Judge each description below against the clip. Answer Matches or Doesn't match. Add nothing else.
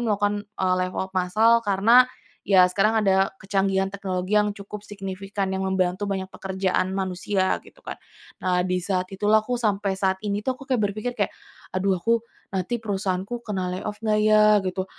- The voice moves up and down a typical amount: Doesn't match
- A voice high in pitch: Matches